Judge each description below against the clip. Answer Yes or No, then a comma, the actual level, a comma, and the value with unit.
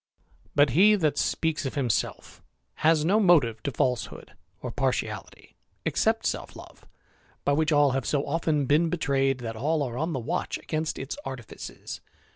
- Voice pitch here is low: No, medium, 145 Hz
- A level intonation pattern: No, average, 3.3 semitones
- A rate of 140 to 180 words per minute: Yes, average, 160 wpm